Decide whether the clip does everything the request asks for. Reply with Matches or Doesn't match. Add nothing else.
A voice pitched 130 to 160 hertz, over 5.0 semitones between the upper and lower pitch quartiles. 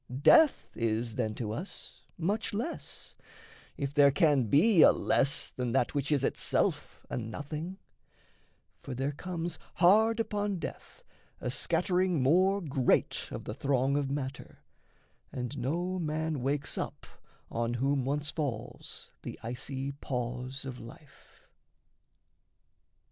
Matches